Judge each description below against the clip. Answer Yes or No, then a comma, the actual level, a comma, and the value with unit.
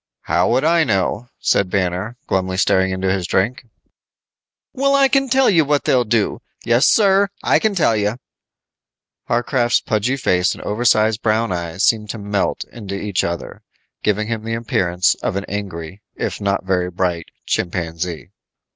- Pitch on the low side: Yes, low, 105 Hz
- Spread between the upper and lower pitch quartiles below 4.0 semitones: No, average, 4.6 semitones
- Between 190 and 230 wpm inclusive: No, average, 160 wpm